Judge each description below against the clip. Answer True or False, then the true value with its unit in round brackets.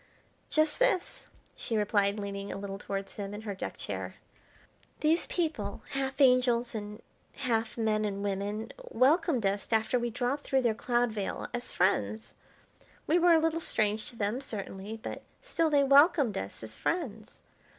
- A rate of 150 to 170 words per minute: True (160 wpm)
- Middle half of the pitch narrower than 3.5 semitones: False (5.3 semitones)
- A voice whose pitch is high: True (225 Hz)